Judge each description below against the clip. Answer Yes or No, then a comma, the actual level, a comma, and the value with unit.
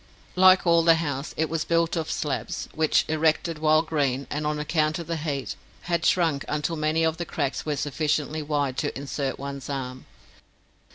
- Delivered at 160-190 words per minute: Yes, average, 180 wpm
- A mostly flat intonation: Yes, narrow, 2.3 semitones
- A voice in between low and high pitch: Yes, medium, 155 Hz